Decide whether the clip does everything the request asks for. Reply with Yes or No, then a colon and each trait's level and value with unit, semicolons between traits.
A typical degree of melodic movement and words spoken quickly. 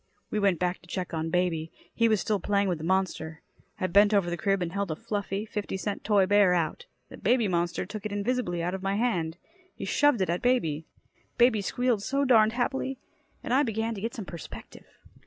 Yes: average, 3.9 semitones; fast, 215 wpm